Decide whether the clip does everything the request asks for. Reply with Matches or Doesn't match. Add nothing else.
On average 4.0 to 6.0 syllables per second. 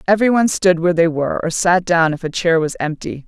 Doesn't match